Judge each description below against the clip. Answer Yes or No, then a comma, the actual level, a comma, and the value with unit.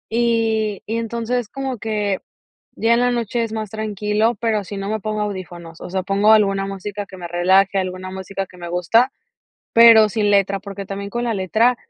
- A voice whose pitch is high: Yes, high, 210 Hz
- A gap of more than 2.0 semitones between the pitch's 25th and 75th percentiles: Yes, average, 2.7 semitones